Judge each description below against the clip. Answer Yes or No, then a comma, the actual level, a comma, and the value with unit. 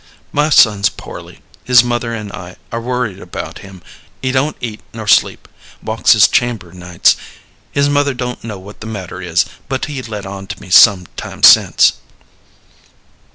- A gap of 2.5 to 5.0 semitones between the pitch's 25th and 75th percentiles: Yes, average, 4.4 semitones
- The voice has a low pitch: Yes, low, 110 Hz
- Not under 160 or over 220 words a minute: Yes, average, 165 wpm